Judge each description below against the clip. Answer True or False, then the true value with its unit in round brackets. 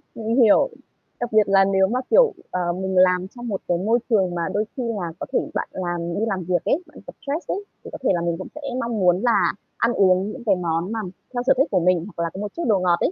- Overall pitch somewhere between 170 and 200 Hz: True (195 Hz)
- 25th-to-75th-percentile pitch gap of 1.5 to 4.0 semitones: False (4.5 semitones)